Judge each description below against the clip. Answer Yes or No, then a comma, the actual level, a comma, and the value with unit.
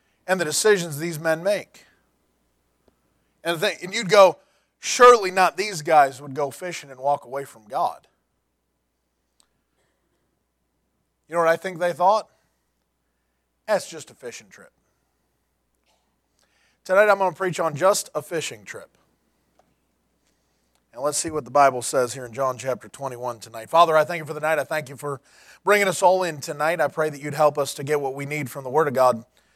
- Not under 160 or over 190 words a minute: Yes, average, 185 wpm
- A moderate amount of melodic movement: No, wide, 6.6 semitones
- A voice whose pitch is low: No, medium, 150 Hz